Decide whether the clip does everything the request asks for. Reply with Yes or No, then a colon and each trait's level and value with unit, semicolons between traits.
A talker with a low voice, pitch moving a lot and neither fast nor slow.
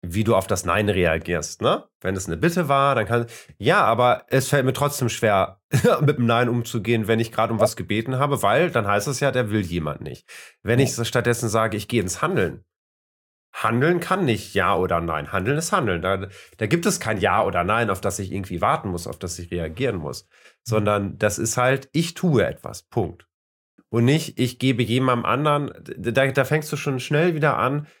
No: low, 115 Hz; wide, 5.8 semitones; fast, 210 wpm